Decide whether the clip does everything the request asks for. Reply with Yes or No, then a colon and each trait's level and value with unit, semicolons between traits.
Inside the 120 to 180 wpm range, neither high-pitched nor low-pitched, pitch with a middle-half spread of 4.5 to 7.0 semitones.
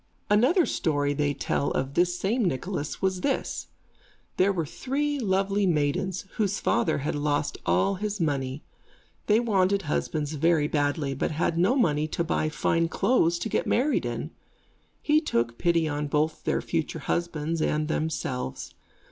Yes: average, 155 wpm; medium, 165 Hz; average, 5.1 semitones